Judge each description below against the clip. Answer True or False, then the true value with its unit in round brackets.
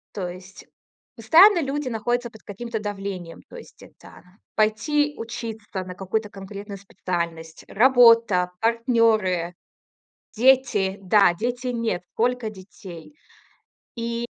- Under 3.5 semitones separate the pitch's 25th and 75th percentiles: False (3.9 semitones)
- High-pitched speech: True (220 Hz)